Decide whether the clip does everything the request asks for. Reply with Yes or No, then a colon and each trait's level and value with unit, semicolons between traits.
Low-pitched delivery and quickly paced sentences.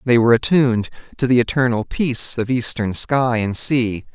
No: low, 120 Hz; average, 175 wpm